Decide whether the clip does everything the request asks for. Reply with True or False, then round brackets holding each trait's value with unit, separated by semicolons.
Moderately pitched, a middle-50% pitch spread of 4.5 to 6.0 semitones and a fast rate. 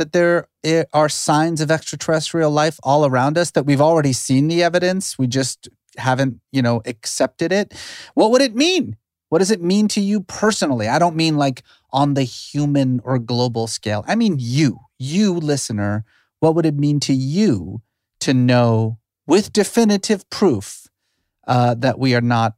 False (145 Hz; 5.5 semitones; 175 wpm)